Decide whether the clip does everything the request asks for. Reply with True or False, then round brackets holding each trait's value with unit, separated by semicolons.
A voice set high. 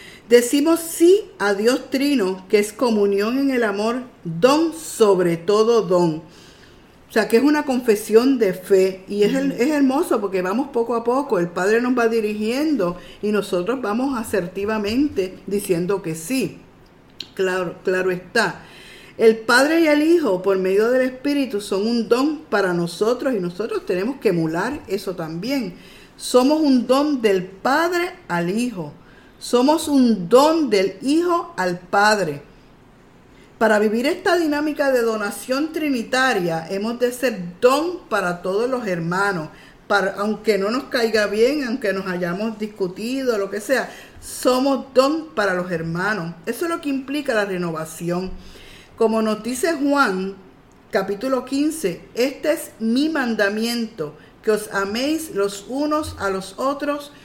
True (225 Hz)